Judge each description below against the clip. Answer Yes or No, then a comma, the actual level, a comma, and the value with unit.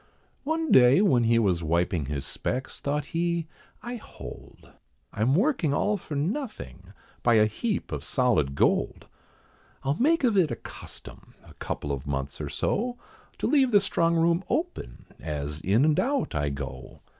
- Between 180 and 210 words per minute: No, average, 165 wpm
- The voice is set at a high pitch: No, medium, 140 Hz